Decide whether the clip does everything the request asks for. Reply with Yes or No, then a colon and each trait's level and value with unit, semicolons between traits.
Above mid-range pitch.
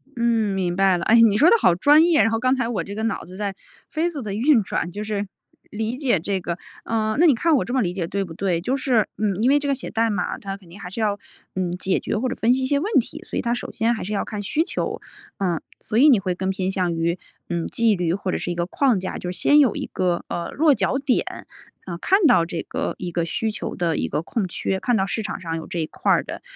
Yes: high, 205 Hz